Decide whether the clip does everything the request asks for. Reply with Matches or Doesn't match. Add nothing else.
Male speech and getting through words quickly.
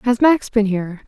Doesn't match